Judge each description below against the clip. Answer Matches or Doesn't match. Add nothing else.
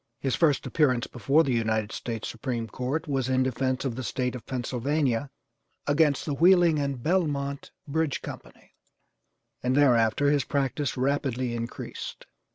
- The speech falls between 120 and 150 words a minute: Matches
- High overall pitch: Doesn't match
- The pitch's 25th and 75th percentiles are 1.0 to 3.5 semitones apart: Matches